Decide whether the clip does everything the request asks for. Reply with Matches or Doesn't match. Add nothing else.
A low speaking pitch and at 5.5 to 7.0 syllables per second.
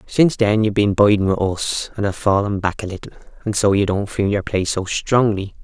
Matches